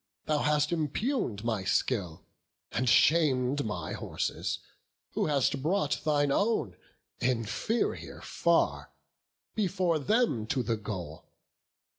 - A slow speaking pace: Yes, slow, 105 wpm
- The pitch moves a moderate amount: No, wide, 6.1 semitones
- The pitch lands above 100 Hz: Yes, medium, 140 Hz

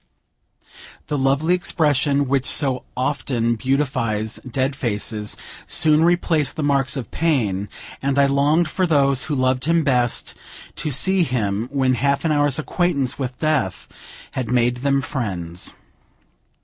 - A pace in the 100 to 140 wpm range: Yes, slow, 135 wpm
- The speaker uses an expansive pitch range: No, average, 3.3 semitones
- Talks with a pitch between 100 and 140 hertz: Yes, low, 135 Hz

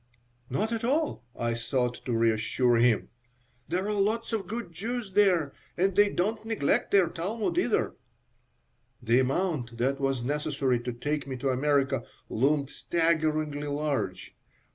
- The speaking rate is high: No, average, 140 wpm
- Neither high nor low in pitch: Yes, medium, 150 Hz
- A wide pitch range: Yes, wide, 7.6 semitones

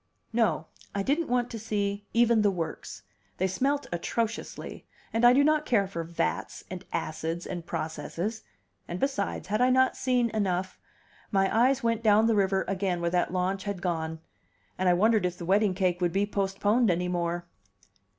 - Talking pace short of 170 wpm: No, average, 180 wpm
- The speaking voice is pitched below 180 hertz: No, high, 200 Hz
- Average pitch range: Yes, average, 4.4 semitones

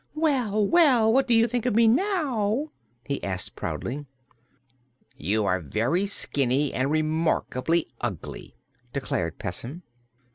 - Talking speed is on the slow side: Yes, slow, 120 wpm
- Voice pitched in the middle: Yes, medium, 170 Hz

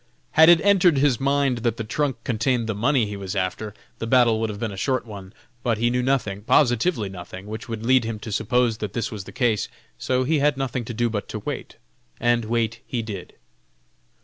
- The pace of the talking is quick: Yes, fast, 220 wpm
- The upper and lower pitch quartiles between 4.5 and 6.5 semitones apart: No, average, 3.3 semitones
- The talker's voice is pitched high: No, low, 115 Hz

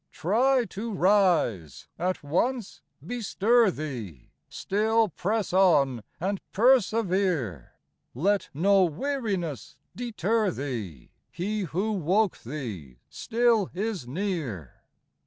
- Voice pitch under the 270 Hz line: Yes, high, 190 Hz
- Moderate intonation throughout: No, wide, 7.2 semitones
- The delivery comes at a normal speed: No, slow, 95 wpm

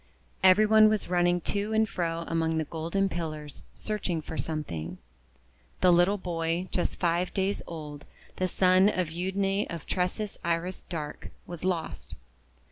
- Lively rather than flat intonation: No, average, 2.8 semitones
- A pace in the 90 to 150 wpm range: Yes, average, 145 wpm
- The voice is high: No, medium, 175 Hz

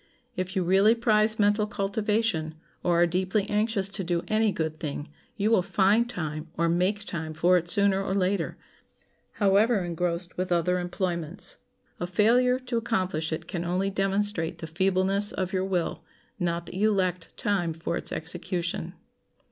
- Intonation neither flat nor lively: Yes, average, 3.1 semitones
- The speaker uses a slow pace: No, average, 165 wpm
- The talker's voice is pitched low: No, medium, 185 Hz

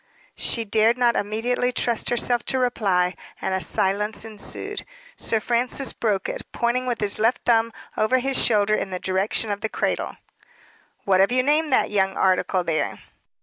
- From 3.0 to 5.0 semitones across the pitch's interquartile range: Yes, average, 3.6 semitones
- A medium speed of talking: Yes, average, 170 wpm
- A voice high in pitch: Yes, high, 220 Hz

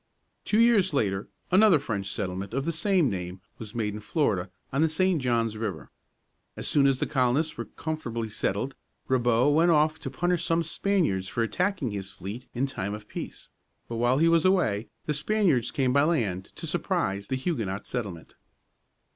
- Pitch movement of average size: No, wide, 7.3 semitones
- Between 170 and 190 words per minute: Yes, average, 180 wpm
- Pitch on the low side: Yes, low, 130 Hz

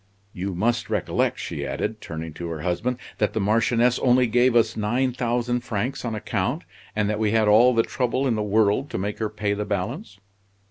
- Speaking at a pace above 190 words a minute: Yes, average, 200 wpm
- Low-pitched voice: Yes, low, 110 Hz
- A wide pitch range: No, average, 3.0 semitones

